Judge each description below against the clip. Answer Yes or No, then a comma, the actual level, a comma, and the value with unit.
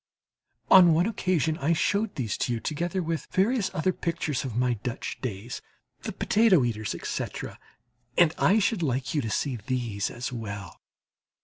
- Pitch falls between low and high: Yes, medium, 150 Hz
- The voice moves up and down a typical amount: No, wide, 7.0 semitones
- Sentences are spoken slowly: No, average, 165 wpm